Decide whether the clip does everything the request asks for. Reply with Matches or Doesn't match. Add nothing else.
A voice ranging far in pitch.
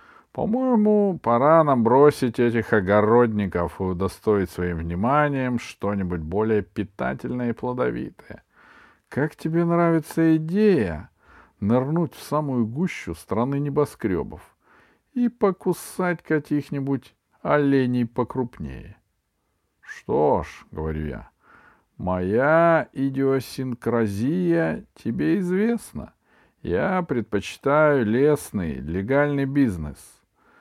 Matches